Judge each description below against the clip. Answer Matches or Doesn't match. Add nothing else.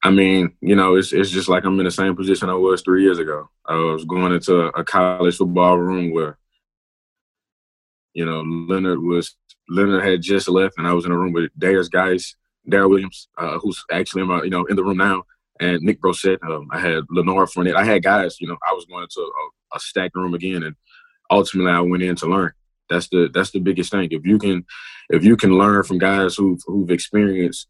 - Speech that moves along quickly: Matches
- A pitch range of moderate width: Doesn't match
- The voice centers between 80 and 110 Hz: Matches